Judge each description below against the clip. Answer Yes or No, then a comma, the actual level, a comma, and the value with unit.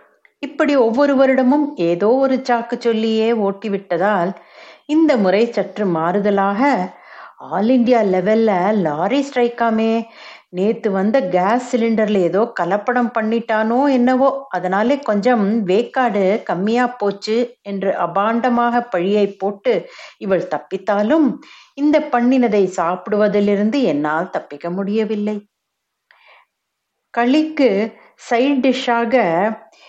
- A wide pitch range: No, average, 4.1 semitones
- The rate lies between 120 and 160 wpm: No, average, 90 wpm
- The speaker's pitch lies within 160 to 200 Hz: No, high, 225 Hz